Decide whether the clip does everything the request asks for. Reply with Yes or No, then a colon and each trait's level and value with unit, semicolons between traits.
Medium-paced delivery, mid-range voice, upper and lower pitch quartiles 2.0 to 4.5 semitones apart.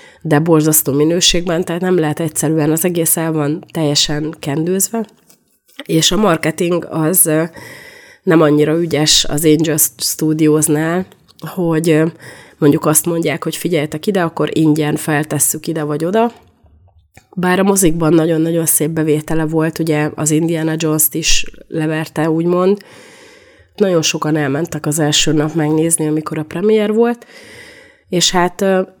Yes: average, 130 wpm; medium, 160 Hz; narrow, 2.5 semitones